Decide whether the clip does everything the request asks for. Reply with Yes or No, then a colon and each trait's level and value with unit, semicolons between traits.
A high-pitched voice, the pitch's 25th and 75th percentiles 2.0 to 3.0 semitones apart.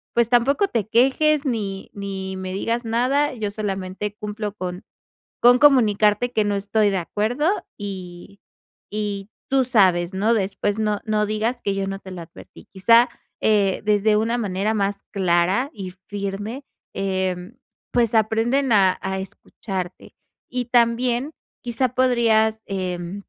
No: high, 210 Hz; average, 3.4 semitones